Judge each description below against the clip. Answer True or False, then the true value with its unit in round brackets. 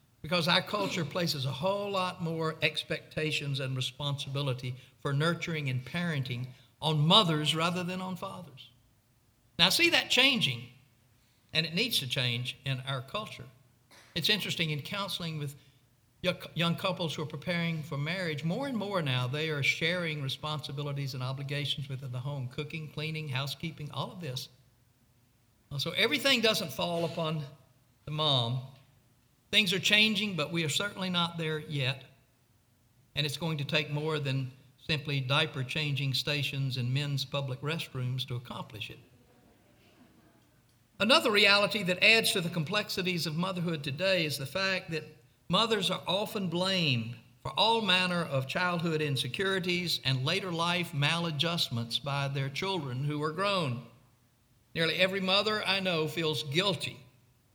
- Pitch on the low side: False (150 Hz)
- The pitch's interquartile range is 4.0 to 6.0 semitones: True (5.2 semitones)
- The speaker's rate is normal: True (145 wpm)